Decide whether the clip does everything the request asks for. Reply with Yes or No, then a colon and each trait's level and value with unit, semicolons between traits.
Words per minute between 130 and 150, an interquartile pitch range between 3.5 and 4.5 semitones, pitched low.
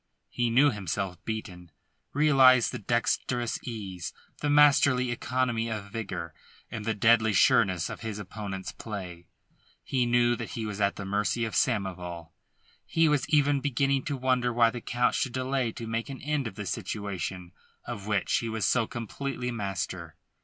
No: average, 165 wpm; average, 4.2 semitones; low, 115 Hz